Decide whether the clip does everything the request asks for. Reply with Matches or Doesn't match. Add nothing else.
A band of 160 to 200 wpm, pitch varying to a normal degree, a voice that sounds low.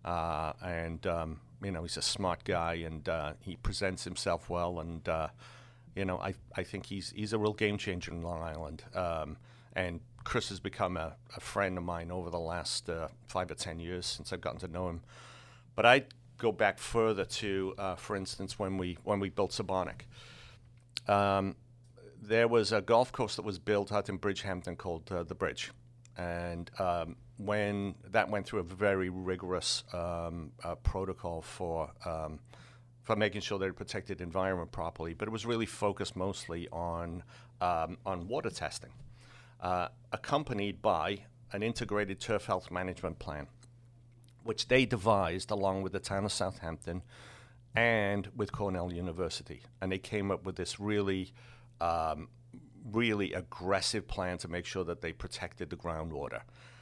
Matches